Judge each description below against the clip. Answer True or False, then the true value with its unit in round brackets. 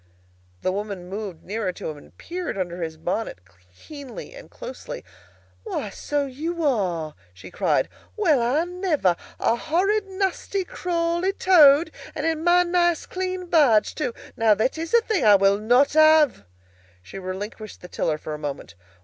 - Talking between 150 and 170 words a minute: True (165 wpm)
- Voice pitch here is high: True (280 Hz)